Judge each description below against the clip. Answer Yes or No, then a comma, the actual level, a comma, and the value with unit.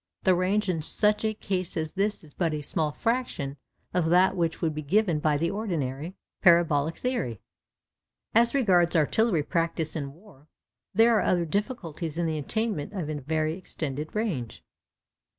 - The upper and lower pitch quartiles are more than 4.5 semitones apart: Yes, average, 4.9 semitones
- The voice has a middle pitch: Yes, medium, 170 Hz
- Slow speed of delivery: No, average, 165 wpm